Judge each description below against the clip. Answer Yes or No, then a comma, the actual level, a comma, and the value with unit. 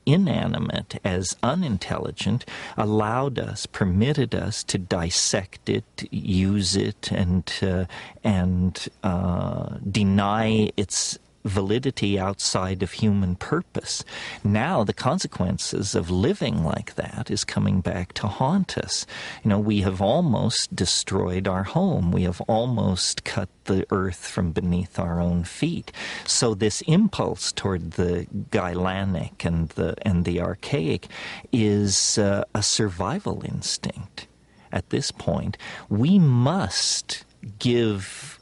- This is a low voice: Yes, low, 100 Hz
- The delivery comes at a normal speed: No, slow, 120 wpm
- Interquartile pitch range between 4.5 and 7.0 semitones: No, average, 3.0 semitones